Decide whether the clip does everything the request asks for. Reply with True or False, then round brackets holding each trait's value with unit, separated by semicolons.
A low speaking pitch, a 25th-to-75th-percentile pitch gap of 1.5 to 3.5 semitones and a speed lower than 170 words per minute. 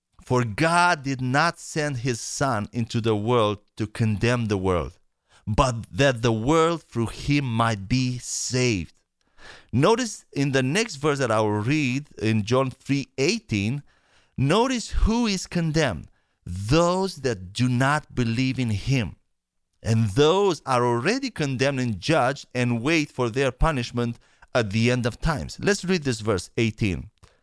False (125 Hz; 4.6 semitones; 150 wpm)